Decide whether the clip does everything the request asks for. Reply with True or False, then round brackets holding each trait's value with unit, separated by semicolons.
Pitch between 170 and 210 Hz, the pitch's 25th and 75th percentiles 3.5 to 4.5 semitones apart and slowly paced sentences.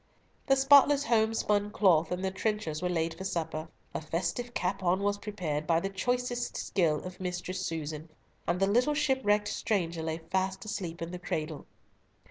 False (185 Hz; 4.2 semitones; 170 wpm)